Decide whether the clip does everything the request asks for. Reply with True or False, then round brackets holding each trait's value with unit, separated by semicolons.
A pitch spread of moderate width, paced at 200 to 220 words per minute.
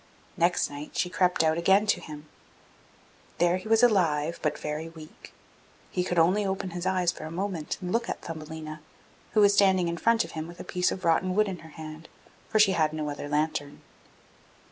True (3.3 semitones; 205 wpm)